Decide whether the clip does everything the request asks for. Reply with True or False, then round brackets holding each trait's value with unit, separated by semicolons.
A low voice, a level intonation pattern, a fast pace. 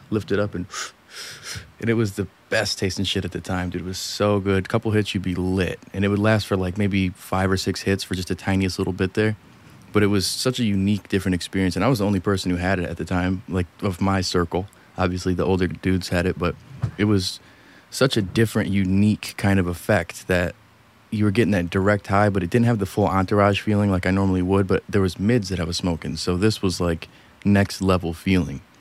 True (95 Hz; 2.1 semitones; 245 wpm)